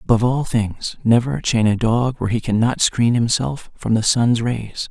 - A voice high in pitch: No, low, 115 Hz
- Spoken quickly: No, average, 195 wpm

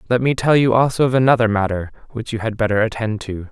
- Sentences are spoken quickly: Yes, fast, 240 wpm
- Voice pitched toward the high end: No, low, 115 Hz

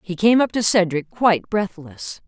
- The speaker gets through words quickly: No, average, 185 wpm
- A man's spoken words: No, female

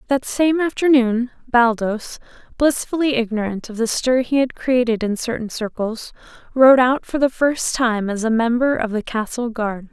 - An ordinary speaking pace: Yes, average, 170 wpm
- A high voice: Yes, high, 240 Hz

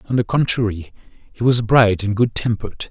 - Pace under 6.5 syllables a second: Yes, 5.4 syllables/s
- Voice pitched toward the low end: Yes, low, 110 Hz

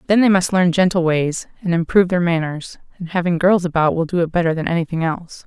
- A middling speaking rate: No, fast, 240 wpm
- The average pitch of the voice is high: No, medium, 175 Hz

